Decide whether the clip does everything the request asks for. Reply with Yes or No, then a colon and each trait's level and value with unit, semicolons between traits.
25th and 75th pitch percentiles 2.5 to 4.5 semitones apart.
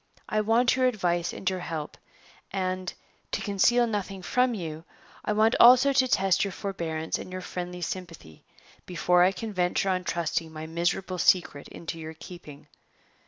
Yes: average, 3.7 semitones